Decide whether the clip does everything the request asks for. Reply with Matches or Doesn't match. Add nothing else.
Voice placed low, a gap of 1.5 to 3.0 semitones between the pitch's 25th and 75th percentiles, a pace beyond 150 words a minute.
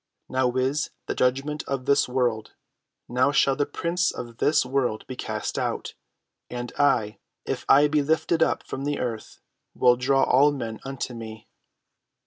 Matches